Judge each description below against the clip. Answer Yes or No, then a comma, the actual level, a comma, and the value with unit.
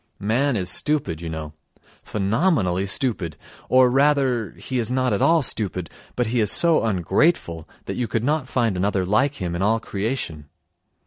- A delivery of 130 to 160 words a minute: No, average, 170 wpm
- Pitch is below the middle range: Yes, low, 110 Hz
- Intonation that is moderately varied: No, wide, 6.1 semitones